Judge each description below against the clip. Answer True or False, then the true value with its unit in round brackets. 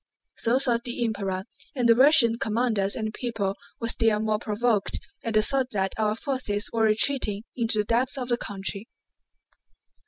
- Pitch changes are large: False (2.5 semitones)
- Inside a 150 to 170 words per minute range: True (165 wpm)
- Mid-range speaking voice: False (225 Hz)